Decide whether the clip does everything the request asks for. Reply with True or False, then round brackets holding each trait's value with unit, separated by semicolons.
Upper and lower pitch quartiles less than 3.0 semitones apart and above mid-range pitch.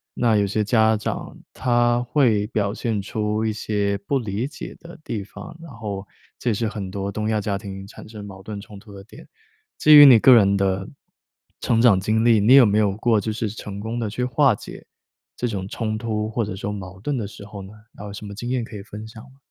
False (2.6 semitones; 110 Hz)